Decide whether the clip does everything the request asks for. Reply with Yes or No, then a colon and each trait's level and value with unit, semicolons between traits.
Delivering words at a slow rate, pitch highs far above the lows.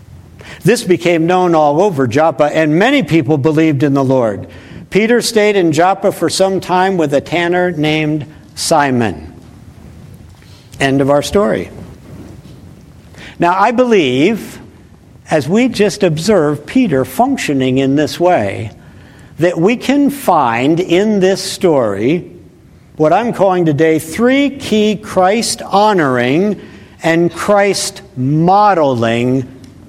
Yes: slow, 120 wpm; wide, 6.6 semitones